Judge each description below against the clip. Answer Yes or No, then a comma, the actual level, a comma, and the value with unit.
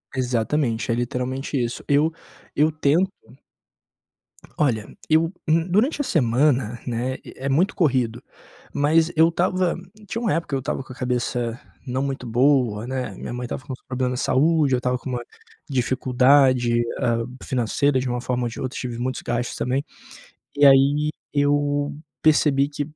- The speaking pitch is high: No, low, 130 Hz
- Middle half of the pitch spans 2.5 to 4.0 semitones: Yes, average, 3.1 semitones